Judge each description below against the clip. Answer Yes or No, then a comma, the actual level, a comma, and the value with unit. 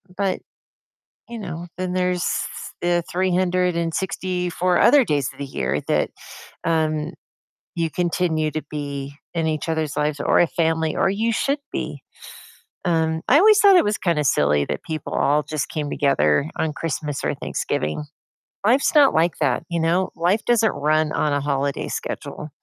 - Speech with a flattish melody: No, average, 3.4 semitones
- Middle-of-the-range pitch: Yes, medium, 165 Hz